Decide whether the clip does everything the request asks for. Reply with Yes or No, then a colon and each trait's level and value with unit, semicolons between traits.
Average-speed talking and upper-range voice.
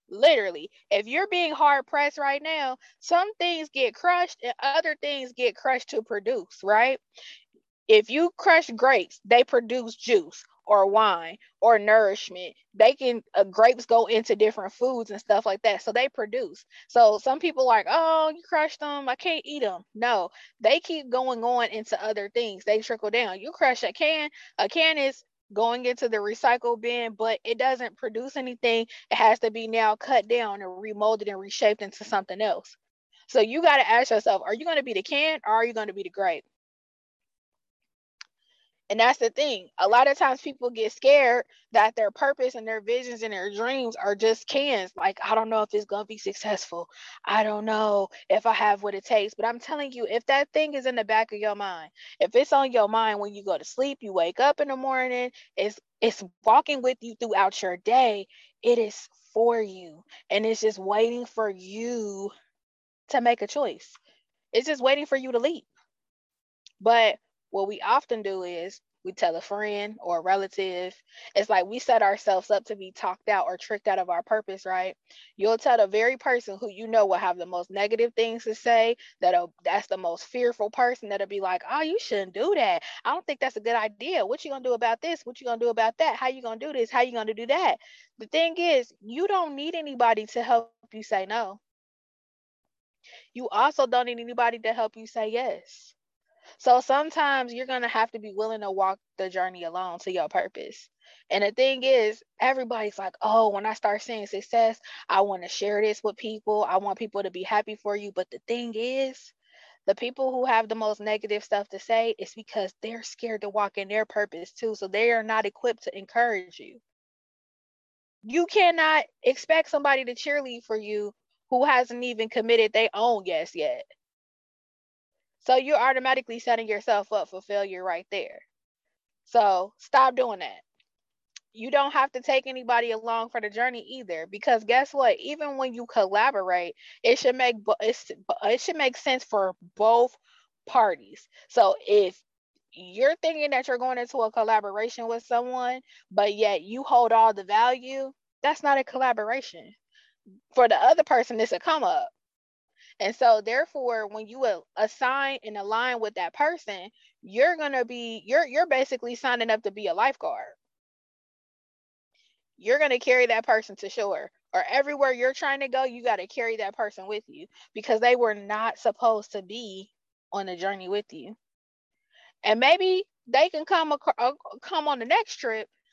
Yes: average, 195 wpm; high, 235 Hz